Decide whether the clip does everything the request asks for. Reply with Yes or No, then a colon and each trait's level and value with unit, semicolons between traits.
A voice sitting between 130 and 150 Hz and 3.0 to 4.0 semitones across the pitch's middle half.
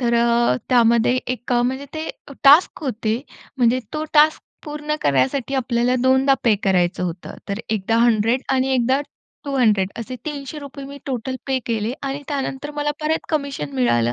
No: very high, 255 Hz; average, 3.7 semitones